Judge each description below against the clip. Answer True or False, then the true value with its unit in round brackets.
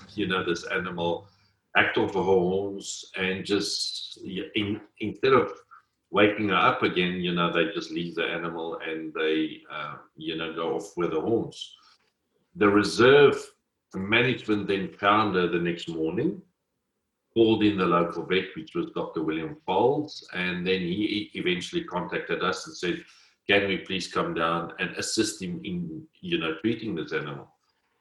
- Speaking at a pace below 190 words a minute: True (160 wpm)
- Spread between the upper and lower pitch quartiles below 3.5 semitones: False (5.0 semitones)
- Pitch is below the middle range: True (95 Hz)